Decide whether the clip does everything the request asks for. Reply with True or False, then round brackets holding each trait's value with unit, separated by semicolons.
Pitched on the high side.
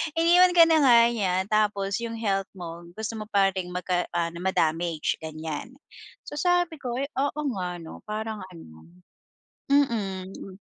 True (200 Hz)